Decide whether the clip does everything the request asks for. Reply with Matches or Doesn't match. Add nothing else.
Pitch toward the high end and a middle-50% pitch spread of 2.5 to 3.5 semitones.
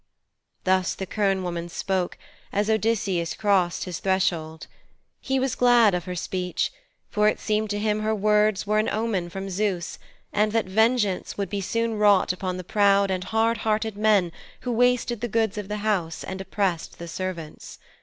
Matches